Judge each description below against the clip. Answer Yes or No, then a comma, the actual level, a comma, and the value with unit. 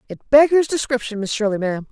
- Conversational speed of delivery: Yes, average, 190 wpm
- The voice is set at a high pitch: Yes, high, 240 Hz